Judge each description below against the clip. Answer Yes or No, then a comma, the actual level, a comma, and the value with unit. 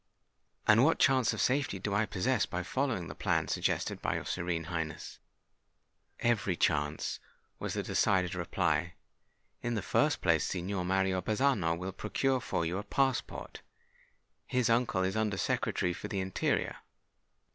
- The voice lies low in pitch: Yes, very low, 95 Hz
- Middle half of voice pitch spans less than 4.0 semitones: No, average, 4.9 semitones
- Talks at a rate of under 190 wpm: Yes, average, 150 wpm